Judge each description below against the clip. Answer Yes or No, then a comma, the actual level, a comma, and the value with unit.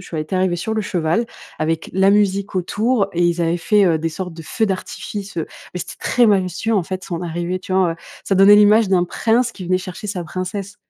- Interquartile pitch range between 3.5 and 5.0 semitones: No, average, 3.0 semitones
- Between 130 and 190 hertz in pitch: Yes, medium, 185 Hz